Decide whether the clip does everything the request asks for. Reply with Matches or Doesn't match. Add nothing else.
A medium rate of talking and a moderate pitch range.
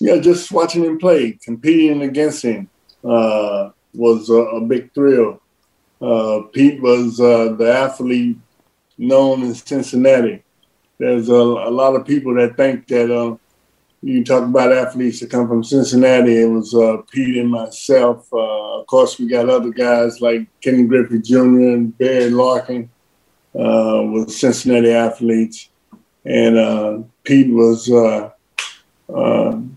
Doesn't match